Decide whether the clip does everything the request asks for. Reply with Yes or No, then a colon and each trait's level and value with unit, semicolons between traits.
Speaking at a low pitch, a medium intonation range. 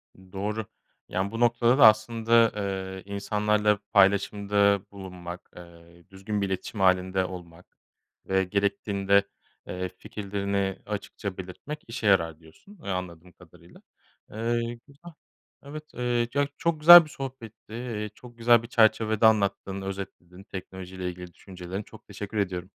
Yes: low, 100 Hz; average, 3.4 semitones